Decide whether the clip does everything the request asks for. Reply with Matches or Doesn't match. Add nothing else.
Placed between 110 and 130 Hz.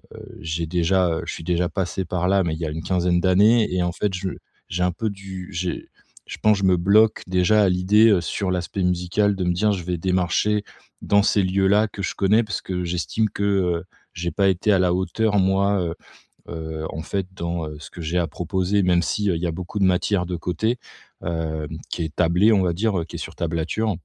Doesn't match